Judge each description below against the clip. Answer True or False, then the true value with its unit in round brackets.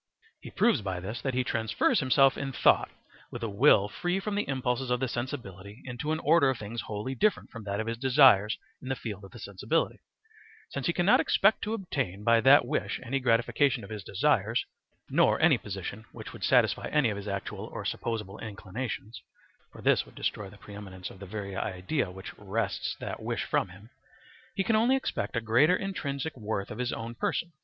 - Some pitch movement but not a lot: True (5.0 semitones)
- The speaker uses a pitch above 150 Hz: False (115 Hz)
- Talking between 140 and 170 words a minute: False (205 wpm)